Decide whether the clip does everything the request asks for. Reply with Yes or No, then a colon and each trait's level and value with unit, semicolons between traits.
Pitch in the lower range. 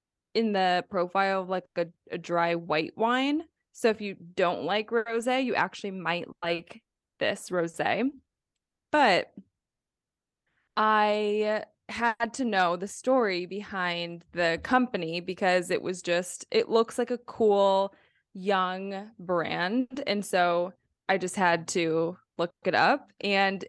No: high, 195 Hz